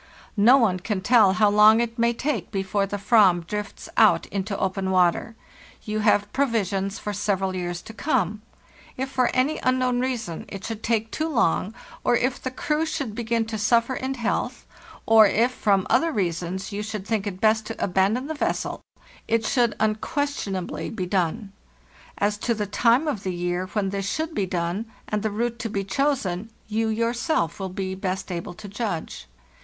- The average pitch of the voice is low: No, high, 215 Hz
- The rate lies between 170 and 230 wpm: Yes, average, 185 wpm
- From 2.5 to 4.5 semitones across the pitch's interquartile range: Yes, average, 3.6 semitones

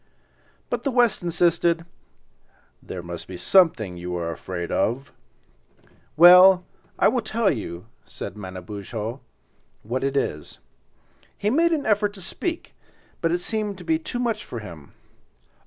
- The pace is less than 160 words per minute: Yes, average, 140 wpm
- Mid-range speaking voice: Yes, medium, 165 Hz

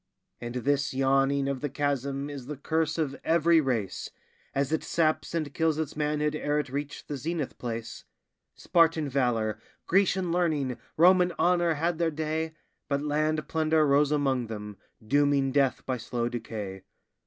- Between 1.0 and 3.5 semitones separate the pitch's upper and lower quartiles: Yes, average, 3.1 semitones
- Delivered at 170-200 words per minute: No, average, 155 wpm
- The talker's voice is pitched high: No, medium, 145 Hz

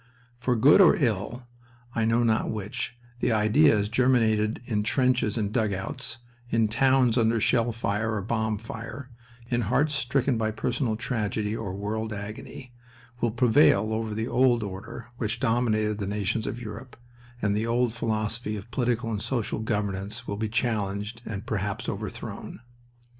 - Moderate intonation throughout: No, narrow, 2.3 semitones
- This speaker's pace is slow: No, average, 155 wpm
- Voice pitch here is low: Yes, low, 110 Hz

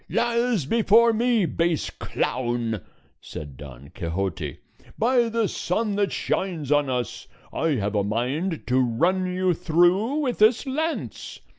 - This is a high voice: No, medium, 175 Hz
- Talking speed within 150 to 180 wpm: No, slow, 135 wpm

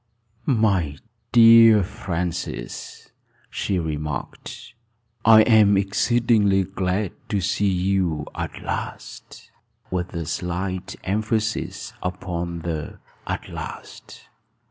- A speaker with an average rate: No, slow, 90 wpm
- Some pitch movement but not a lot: Yes, average, 3.7 semitones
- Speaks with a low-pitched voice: Yes, very low, 95 Hz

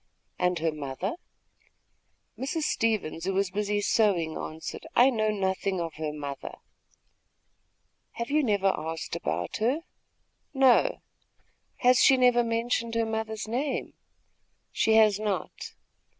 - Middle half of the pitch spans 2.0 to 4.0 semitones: No, average, 5.0 semitones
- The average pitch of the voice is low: No, high, 215 Hz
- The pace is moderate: No, slow, 120 wpm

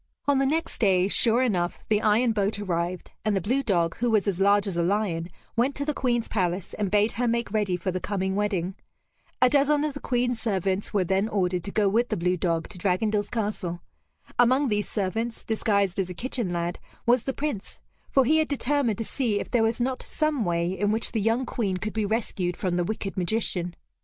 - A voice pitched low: No, high, 210 Hz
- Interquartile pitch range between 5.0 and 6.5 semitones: No, average, 4.4 semitones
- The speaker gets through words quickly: Yes, fast, 220 wpm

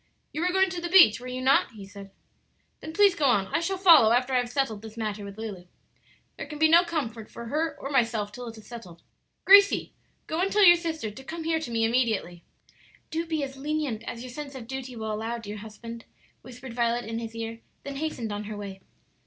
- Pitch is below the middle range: No, high, 245 Hz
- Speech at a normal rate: No, fast, 230 wpm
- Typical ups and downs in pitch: No, wide, 6.1 semitones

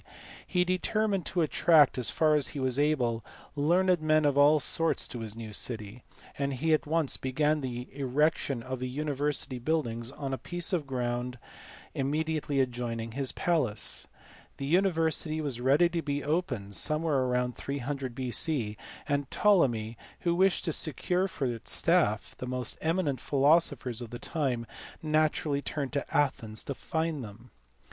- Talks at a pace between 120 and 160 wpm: Yes, average, 155 wpm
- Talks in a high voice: No, medium, 140 Hz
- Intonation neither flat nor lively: Yes, average, 4.1 semitones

